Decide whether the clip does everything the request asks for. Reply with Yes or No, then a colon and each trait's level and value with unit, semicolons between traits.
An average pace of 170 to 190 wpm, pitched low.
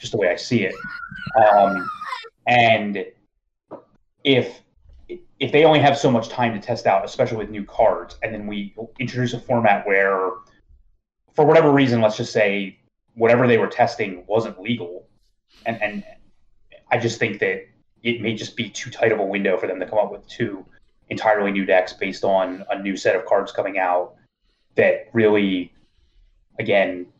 Yes: average, 175 wpm; low, 110 Hz